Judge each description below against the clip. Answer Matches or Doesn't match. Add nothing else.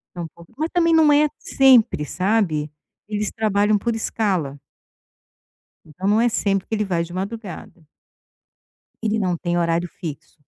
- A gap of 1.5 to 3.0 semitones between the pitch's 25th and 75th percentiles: Doesn't match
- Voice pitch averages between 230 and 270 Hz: Doesn't match